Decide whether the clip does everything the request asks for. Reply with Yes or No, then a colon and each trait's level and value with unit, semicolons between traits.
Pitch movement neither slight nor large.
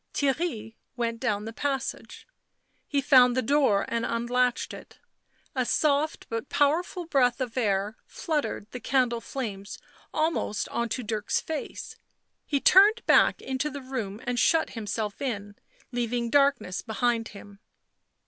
Yes: average, 4.0 semitones